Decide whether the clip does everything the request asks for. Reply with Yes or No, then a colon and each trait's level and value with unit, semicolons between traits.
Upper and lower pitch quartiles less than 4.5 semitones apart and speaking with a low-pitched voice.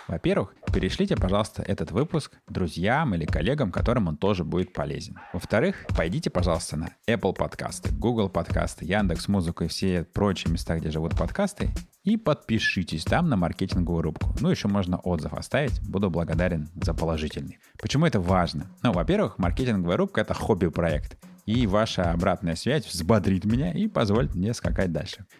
Yes: average, 4.0 semitones; very low, 95 Hz